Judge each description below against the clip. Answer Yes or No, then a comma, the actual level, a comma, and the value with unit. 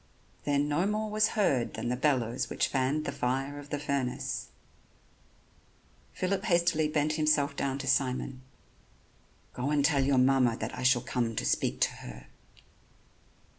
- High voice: No, medium, 140 Hz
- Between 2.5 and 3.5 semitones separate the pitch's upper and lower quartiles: Yes, average, 3.1 semitones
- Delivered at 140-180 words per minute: Yes, average, 155 wpm